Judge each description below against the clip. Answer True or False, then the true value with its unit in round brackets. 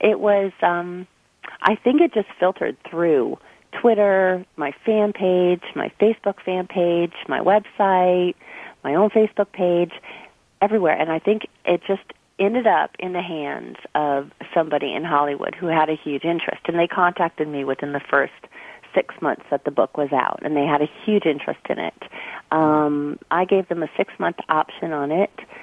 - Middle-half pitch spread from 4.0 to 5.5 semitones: True (4.5 semitones)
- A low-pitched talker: False (175 Hz)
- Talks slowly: False (175 wpm)